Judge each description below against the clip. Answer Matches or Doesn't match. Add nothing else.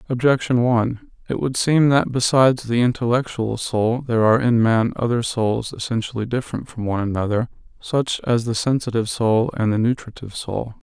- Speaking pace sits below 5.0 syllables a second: Doesn't match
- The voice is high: Doesn't match